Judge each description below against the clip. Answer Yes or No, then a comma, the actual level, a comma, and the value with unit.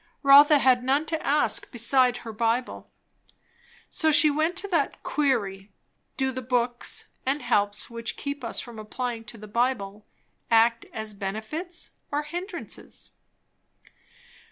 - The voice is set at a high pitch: Yes, very high, 250 Hz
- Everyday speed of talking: No, slow, 130 wpm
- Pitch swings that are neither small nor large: Yes, average, 4.5 semitones